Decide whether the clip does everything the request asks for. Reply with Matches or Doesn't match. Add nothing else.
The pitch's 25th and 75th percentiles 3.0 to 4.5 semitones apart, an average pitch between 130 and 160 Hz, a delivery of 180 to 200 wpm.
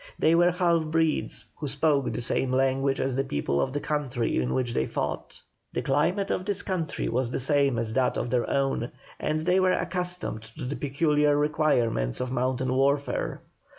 Matches